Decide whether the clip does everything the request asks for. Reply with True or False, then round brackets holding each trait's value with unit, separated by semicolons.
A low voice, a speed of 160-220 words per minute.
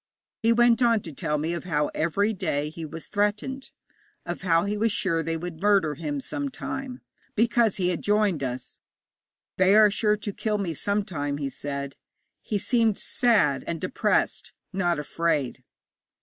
False (185 Hz; 170 wpm)